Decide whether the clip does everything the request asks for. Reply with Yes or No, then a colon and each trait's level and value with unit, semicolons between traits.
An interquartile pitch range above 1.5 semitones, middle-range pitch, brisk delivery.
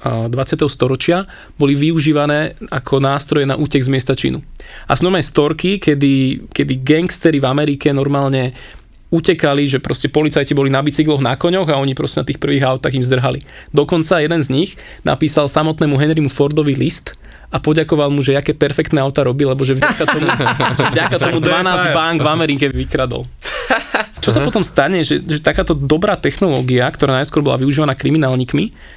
Yes: average, 2.7 semitones; medium, 145 Hz; fast, 170 wpm